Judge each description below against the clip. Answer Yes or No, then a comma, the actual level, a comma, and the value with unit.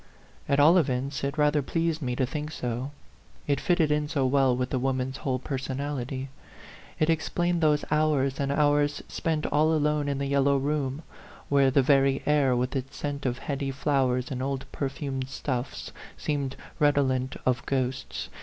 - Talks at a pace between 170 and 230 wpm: Yes, average, 175 wpm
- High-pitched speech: No, medium, 140 Hz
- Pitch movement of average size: No, narrow, 2.0 semitones